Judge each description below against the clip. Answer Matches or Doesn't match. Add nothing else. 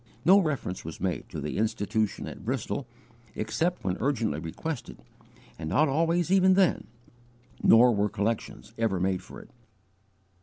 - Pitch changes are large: Matches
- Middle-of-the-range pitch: Doesn't match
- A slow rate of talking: Doesn't match